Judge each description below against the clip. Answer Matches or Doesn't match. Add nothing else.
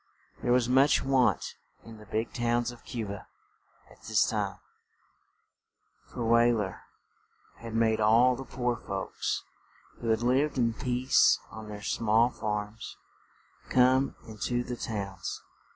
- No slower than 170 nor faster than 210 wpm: Doesn't match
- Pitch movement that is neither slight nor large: Doesn't match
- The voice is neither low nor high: Doesn't match